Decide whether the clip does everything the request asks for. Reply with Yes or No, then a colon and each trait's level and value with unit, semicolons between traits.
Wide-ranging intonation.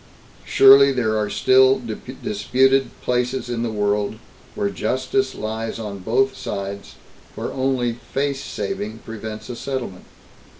No: average, 3.6 semitones